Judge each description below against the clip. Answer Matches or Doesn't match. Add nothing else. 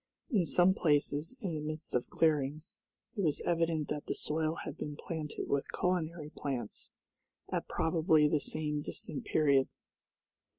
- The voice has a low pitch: Doesn't match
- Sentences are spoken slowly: Doesn't match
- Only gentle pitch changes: Matches